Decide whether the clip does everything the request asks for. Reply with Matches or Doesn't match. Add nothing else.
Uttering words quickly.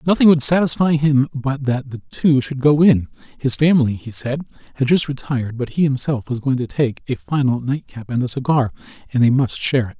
Matches